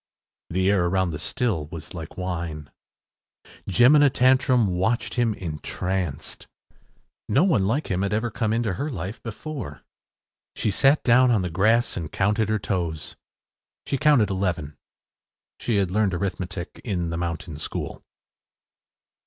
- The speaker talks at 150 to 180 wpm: No, average, 140 wpm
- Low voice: Yes, very low, 95 Hz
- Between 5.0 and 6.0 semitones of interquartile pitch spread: Yes, average, 5.3 semitones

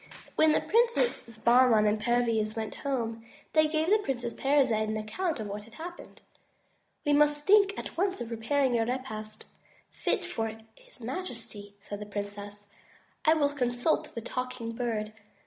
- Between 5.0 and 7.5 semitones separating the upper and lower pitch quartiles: Yes, average, 5.3 semitones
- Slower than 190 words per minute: Yes, average, 160 wpm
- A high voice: Yes, high, 240 Hz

